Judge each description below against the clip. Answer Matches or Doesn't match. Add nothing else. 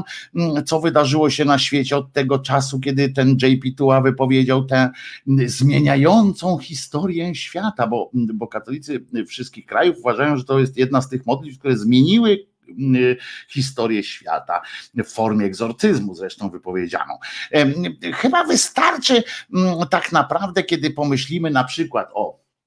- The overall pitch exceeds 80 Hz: Matches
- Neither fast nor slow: Matches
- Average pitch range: Matches